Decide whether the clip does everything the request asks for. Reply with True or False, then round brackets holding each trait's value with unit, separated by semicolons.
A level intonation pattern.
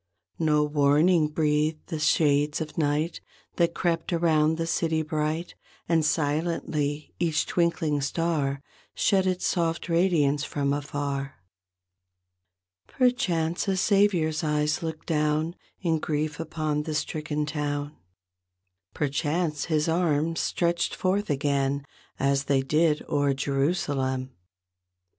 True (2.3 semitones)